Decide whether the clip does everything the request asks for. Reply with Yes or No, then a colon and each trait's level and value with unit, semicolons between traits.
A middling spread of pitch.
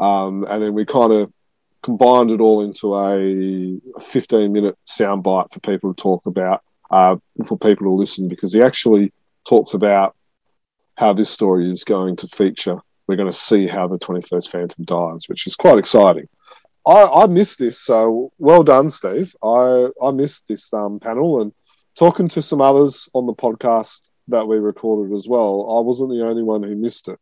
Yes: average, 3.8 semitones